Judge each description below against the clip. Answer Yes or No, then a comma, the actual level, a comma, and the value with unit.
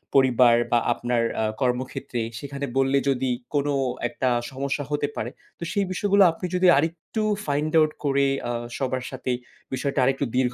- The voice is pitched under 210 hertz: Yes, low, 135 Hz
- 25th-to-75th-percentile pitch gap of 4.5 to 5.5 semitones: No, narrow, 2.4 semitones